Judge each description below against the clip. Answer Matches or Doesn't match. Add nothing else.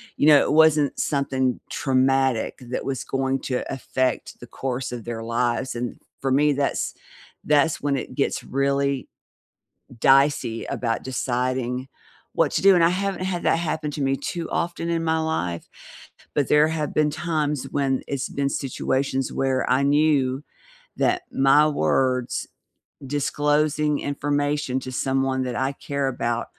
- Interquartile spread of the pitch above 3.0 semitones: Doesn't match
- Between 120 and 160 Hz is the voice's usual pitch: Matches